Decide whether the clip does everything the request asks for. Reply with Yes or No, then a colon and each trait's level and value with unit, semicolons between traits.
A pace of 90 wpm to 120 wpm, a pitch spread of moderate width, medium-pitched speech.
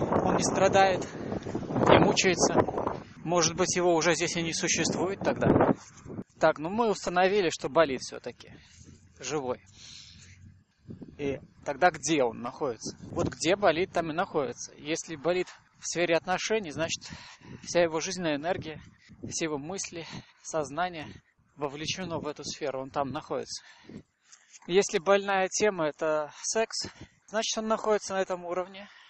No: average, 130 wpm; average, 4.0 semitones; medium, 165 Hz